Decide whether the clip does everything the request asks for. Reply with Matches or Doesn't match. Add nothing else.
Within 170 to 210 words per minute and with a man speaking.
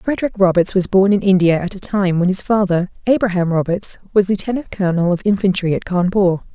Doesn't match